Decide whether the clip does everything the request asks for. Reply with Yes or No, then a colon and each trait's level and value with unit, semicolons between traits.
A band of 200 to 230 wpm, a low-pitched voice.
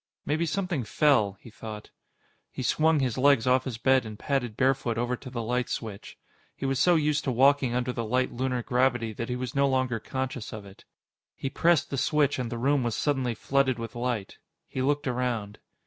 Yes: fast, 205 wpm; low, 125 Hz